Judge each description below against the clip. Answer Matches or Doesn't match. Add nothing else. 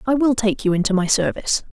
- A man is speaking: Doesn't match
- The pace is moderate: Doesn't match